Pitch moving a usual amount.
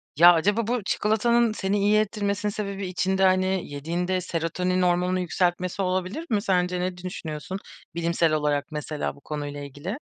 Yes: average, 3.0 semitones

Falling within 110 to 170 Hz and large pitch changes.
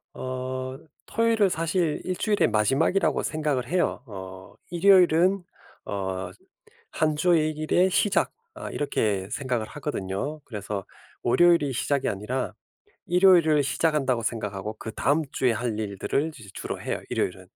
Yes: medium, 140 Hz; wide, 7.5 semitones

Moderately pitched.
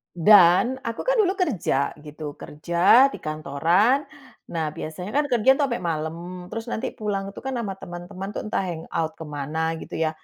Yes: medium, 180 Hz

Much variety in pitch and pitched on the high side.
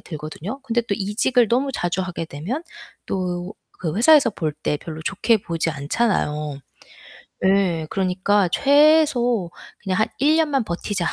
Yes: wide, 6.3 semitones; high, 195 Hz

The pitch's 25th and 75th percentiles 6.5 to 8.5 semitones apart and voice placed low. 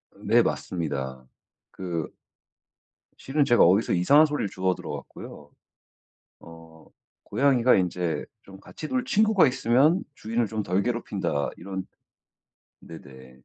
Yes: wide, 7.7 semitones; very low, 95 Hz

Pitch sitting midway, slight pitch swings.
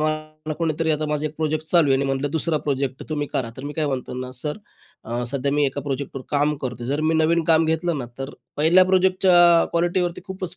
No: medium, 155 Hz; average, 3.0 semitones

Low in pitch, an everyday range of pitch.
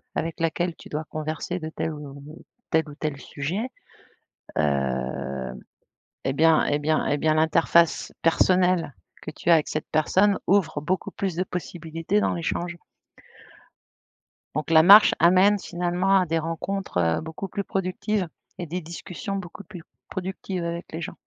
No: medium, 165 Hz; average, 3.0 semitones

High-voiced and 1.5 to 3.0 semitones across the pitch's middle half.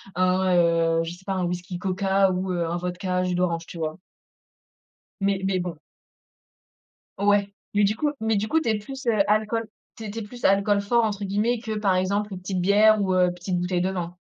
Yes: high, 195 Hz; narrow, 2.6 semitones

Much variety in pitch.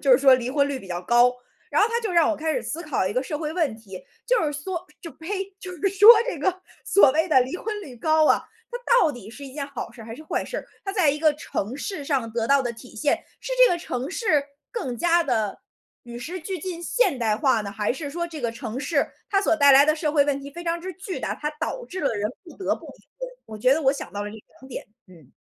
Yes: wide, 5.9 semitones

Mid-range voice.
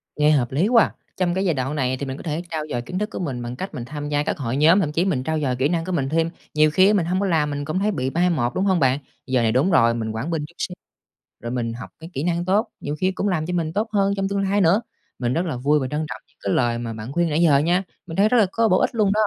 Yes: medium, 155 Hz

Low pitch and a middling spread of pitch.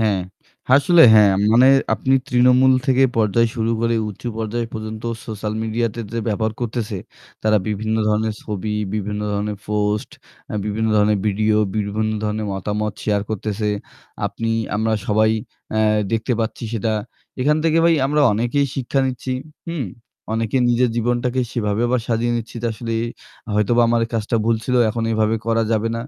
No: low, 110 Hz; narrow, 2.0 semitones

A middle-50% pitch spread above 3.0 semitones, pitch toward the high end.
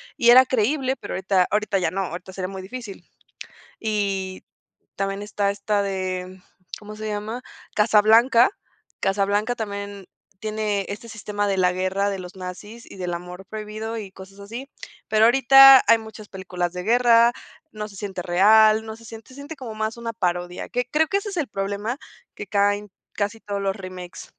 No: average, 2.7 semitones; high, 205 Hz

